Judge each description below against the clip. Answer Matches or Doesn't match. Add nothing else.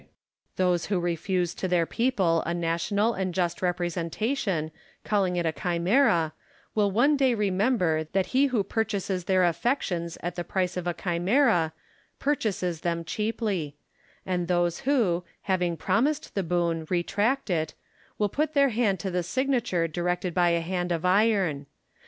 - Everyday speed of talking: Matches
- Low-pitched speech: Doesn't match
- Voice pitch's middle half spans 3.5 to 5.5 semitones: Matches